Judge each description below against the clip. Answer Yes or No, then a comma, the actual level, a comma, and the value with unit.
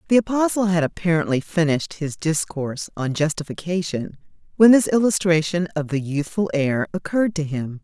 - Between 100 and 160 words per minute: Yes, average, 145 wpm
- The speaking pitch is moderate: Yes, medium, 170 Hz